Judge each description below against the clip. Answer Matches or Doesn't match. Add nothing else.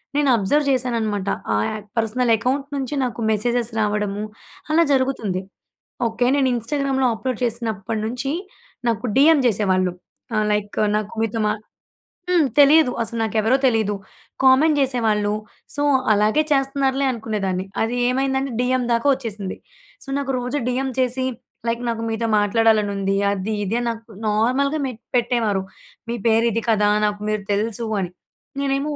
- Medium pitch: Doesn't match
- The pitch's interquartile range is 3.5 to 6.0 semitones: Matches